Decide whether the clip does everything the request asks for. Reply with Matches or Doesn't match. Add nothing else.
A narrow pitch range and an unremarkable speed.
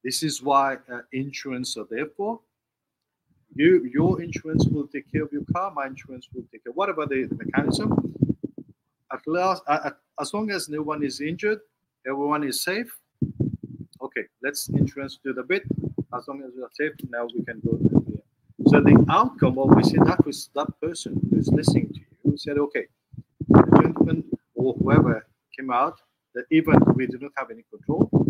Doesn't match